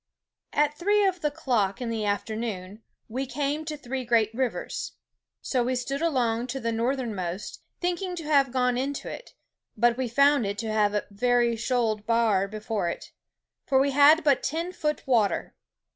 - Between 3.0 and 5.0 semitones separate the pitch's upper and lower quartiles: Yes, average, 4.3 semitones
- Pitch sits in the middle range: No, high, 245 Hz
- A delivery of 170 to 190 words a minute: Yes, average, 175 wpm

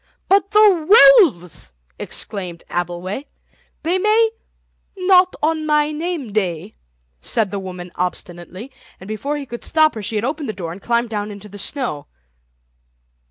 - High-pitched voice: Yes, high, 235 Hz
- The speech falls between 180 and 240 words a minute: No, average, 150 wpm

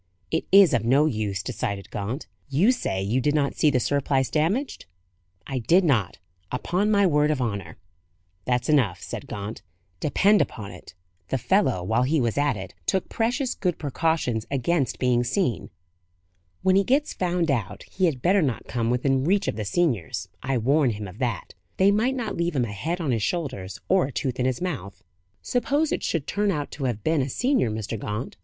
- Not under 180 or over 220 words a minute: Yes, average, 195 wpm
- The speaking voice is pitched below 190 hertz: Yes, low, 135 Hz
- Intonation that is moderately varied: No, wide, 7.6 semitones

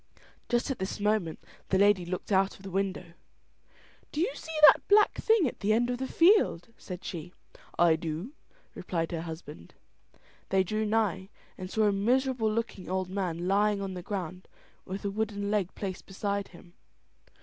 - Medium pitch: No, high, 195 Hz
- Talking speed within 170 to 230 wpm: Yes, average, 175 wpm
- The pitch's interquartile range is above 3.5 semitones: No, average, 3.2 semitones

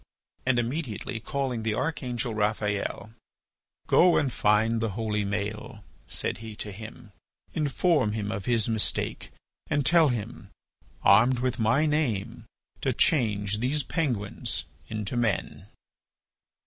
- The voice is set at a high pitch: No, low, 115 Hz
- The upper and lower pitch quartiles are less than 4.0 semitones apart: Yes, average, 3.6 semitones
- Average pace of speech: No, slow, 120 wpm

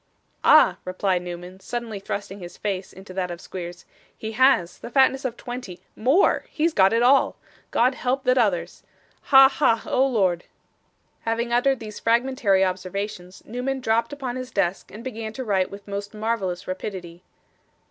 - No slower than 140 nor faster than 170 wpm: Yes, average, 160 wpm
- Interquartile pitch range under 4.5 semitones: No, average, 5.0 semitones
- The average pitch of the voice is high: Yes, high, 215 Hz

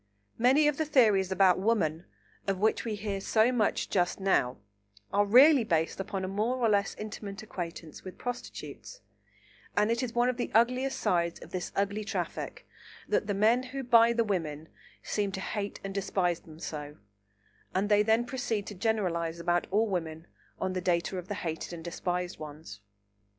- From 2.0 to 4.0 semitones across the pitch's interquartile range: No, average, 4.5 semitones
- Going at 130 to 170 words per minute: No, average, 180 wpm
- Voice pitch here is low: No, high, 200 Hz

